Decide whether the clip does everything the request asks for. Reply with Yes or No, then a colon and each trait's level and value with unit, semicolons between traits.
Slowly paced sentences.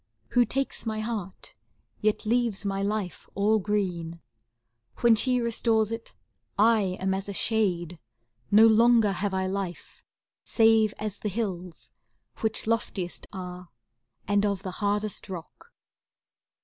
Yes: slow, 130 wpm